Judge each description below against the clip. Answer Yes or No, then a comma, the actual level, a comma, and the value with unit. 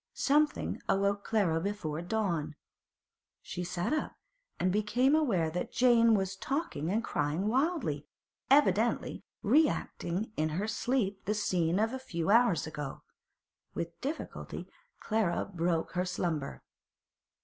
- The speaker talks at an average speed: No, slow, 125 wpm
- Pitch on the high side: Yes, high, 195 Hz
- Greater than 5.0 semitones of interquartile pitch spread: Yes, wide, 5.5 semitones